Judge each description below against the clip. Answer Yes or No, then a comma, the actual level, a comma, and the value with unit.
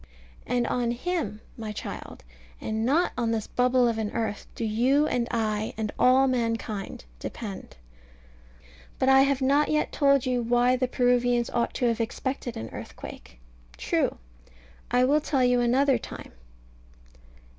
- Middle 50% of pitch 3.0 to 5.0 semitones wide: No, narrow, 2.6 semitones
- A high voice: Yes, high, 245 Hz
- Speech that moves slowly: No, average, 150 wpm